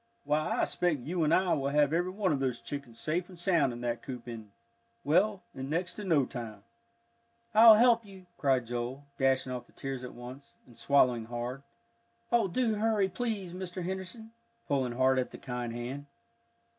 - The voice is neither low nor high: Yes, medium, 145 Hz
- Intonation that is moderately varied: No, wide, 6.7 semitones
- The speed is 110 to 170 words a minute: No, average, 185 wpm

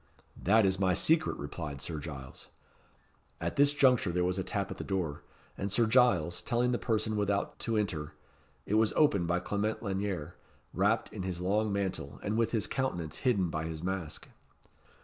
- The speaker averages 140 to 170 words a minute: No, average, 180 wpm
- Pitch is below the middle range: Yes, very low, 95 Hz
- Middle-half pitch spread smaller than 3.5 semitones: No, average, 4.1 semitones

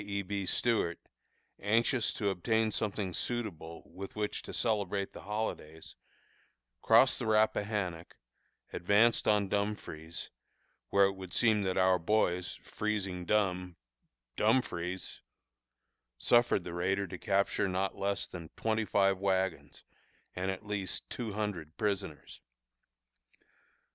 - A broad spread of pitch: No, average, 2.7 semitones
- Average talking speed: No, slow, 120 wpm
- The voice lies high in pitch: No, low, 100 Hz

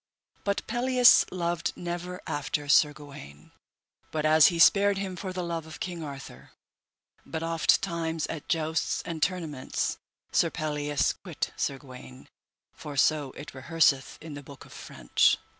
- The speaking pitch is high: No, medium, 160 Hz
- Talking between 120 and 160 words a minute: Yes, average, 145 wpm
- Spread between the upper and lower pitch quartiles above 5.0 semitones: No, average, 3.1 semitones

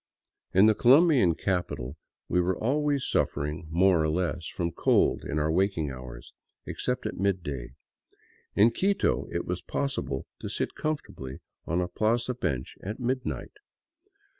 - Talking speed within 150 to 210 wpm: No, average, 140 wpm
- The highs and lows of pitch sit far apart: Yes, wide, 7.5 semitones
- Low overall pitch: Yes, very low, 90 Hz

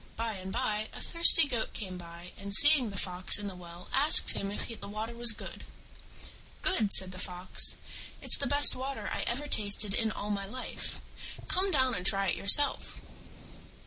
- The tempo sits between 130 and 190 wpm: Yes, average, 185 wpm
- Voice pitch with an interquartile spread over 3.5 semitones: Yes, average, 5.1 semitones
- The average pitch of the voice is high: Yes, high, 210 Hz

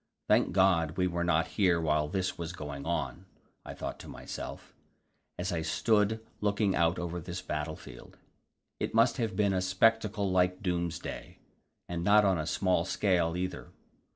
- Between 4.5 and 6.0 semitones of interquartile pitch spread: No, average, 2.8 semitones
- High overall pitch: No, very low, 90 Hz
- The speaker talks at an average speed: Yes, average, 160 wpm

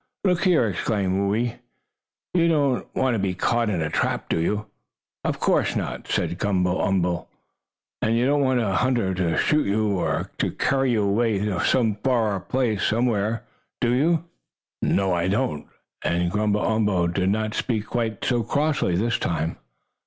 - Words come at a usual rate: Yes, average, 165 wpm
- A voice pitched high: No, low, 110 Hz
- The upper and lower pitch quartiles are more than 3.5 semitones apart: Yes, average, 4.3 semitones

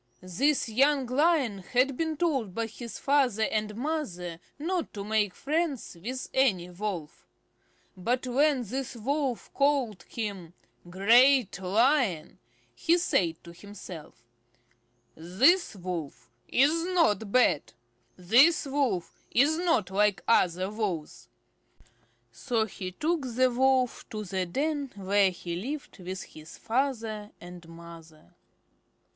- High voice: Yes, high, 225 Hz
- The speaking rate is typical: No, slow, 120 wpm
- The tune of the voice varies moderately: No, wide, 7.0 semitones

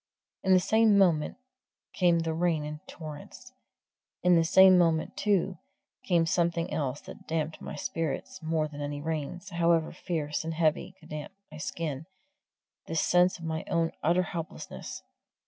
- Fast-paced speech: No, average, 155 wpm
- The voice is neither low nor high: Yes, medium, 165 Hz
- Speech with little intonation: Yes, narrow, 2.3 semitones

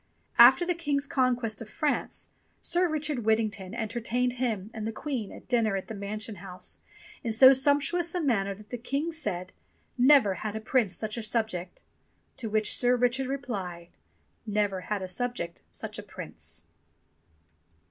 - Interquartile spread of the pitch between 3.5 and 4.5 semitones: Yes, average, 4.2 semitones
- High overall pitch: Yes, high, 230 Hz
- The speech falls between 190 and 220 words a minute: No, average, 160 wpm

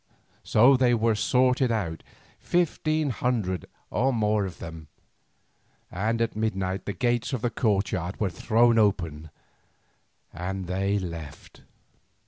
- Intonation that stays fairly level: No, average, 4.6 semitones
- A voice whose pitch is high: No, low, 105 Hz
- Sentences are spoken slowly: Yes, slow, 120 wpm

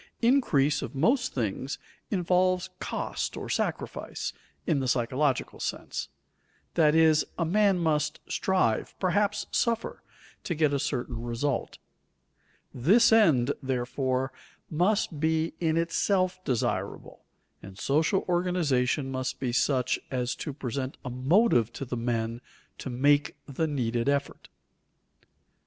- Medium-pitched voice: Yes, medium, 145 Hz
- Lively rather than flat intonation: Yes, wide, 5.7 semitones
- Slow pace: Yes, slow, 120 wpm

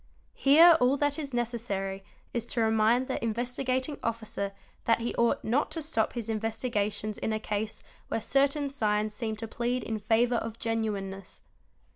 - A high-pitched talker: Yes, high, 230 Hz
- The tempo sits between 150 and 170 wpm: Yes, average, 160 wpm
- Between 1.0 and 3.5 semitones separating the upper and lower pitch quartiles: Yes, average, 2.7 semitones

